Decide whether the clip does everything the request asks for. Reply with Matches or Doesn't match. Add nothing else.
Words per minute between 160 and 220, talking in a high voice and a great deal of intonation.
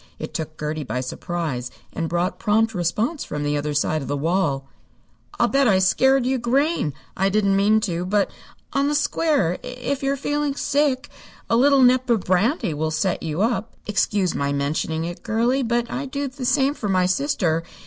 Matches